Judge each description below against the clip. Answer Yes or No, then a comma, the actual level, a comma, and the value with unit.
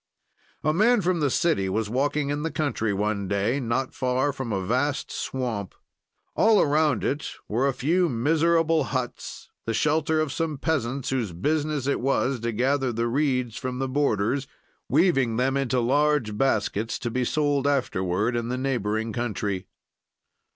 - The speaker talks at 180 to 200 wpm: No, average, 160 wpm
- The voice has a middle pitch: No, low, 130 Hz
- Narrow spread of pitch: No, average, 4.2 semitones